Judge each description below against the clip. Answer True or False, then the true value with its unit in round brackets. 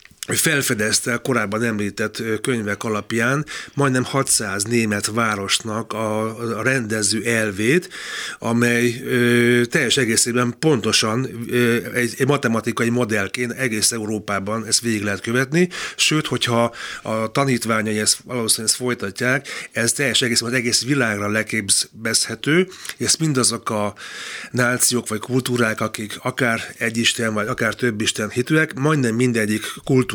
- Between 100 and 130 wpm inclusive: True (110 wpm)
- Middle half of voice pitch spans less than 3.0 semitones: True (2.4 semitones)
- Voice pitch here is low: True (115 Hz)